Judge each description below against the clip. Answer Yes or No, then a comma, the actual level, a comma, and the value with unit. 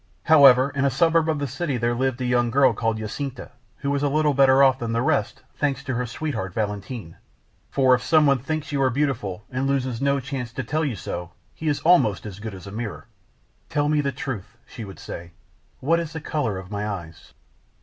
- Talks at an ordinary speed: No, fast, 220 wpm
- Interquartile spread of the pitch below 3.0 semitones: No, average, 4.2 semitones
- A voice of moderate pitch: No, low, 130 Hz